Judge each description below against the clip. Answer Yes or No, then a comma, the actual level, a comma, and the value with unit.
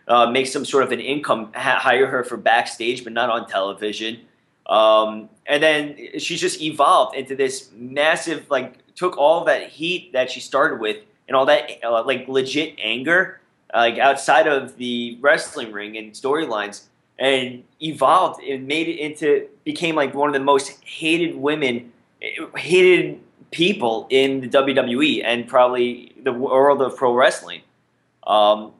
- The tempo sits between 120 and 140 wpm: No, average, 160 wpm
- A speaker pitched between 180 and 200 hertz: No, low, 135 Hz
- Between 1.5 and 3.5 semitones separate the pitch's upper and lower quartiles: No, average, 3.9 semitones